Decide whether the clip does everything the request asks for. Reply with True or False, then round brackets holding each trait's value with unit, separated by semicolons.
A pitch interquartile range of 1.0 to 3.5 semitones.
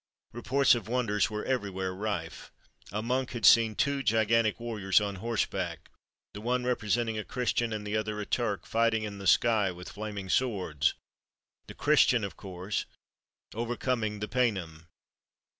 True (2.9 semitones)